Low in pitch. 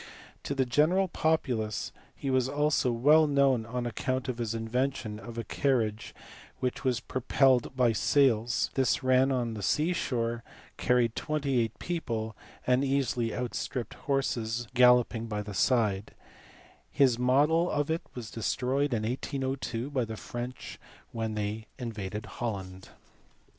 Yes: low, 125 Hz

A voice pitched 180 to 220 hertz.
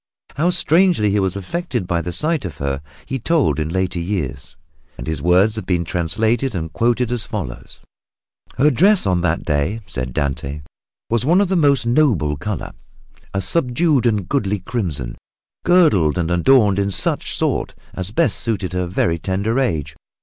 No: low, 100 Hz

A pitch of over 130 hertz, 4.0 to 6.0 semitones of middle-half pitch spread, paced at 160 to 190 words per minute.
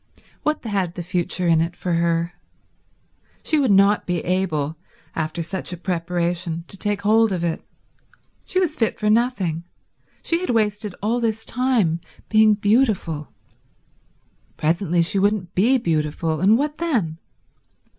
No: high, 190 Hz; average, 4.7 semitones; average, 145 wpm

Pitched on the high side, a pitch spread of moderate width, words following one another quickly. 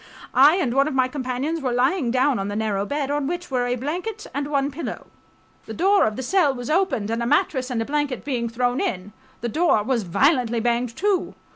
Yes: very high, 260 Hz; average, 4.1 semitones; fast, 225 wpm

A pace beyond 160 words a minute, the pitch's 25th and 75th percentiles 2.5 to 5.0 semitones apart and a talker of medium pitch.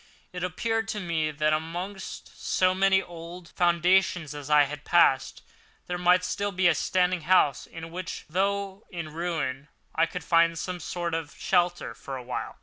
Yes: average, 170 wpm; average, 2.8 semitones; medium, 175 Hz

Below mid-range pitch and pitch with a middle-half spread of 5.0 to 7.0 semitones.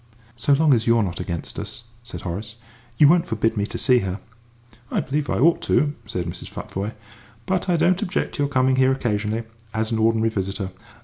Yes: low, 115 Hz; average, 5.3 semitones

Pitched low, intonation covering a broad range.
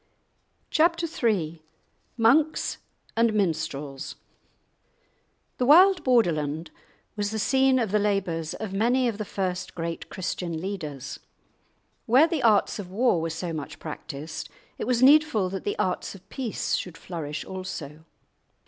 No: high, 195 Hz; wide, 6.7 semitones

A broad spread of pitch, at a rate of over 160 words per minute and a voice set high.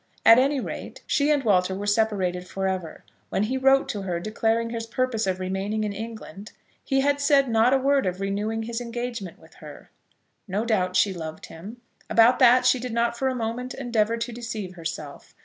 No: average, 4.3 semitones; average, 200 wpm; high, 225 Hz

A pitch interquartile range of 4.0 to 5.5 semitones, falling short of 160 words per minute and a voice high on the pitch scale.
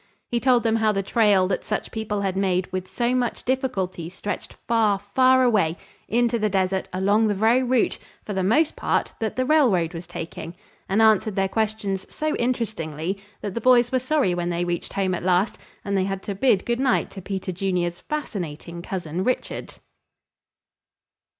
No: average, 4.3 semitones; average, 180 wpm; high, 200 Hz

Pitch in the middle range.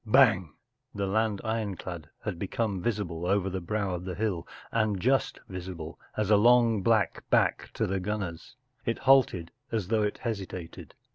No: low, 100 Hz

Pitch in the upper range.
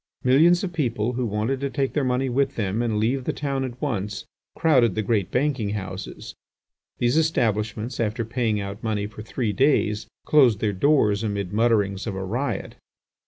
No: low, 115 Hz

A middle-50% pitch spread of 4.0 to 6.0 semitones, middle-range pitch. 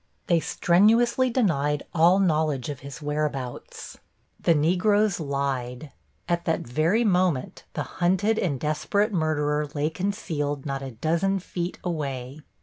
Yes: average, 4.5 semitones; medium, 155 Hz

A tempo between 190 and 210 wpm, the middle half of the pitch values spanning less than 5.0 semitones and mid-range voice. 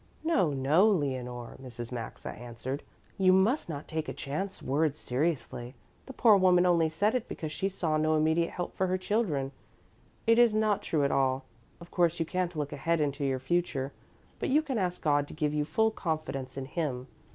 No: average, 195 wpm; average, 5.3 semitones; medium, 160 Hz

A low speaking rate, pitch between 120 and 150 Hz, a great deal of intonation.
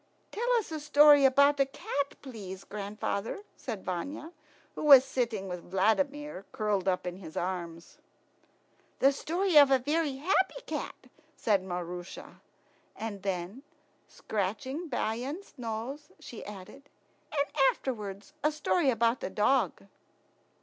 No: slow, 130 wpm; high, 245 Hz; wide, 6.8 semitones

